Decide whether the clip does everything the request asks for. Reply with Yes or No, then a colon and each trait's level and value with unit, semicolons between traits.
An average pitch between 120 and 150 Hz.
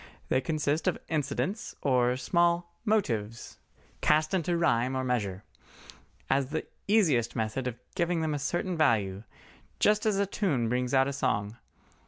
Yes: medium, 140 Hz